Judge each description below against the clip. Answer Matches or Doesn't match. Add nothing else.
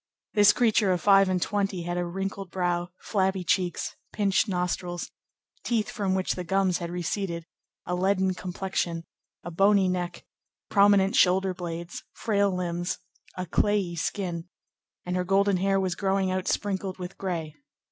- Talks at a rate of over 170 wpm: Doesn't match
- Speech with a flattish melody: Matches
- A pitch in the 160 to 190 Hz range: Matches